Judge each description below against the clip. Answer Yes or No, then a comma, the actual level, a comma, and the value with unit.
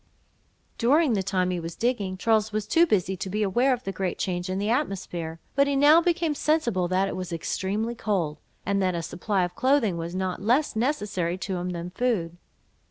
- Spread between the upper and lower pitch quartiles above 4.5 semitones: Yes, average, 5.1 semitones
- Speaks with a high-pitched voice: Yes, high, 195 Hz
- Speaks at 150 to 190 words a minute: No, fast, 205 wpm